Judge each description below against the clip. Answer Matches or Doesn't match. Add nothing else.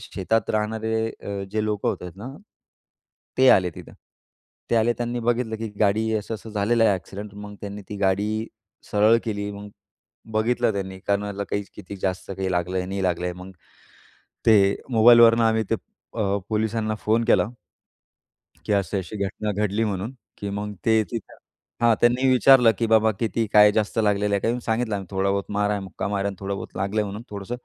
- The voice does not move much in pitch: Matches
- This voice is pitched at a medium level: Doesn't match